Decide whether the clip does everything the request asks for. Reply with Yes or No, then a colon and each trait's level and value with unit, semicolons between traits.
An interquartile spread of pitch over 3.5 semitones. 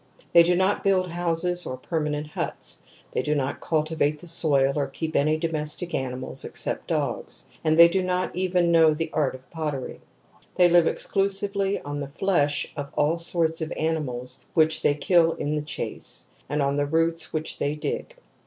No: average, 3.0 semitones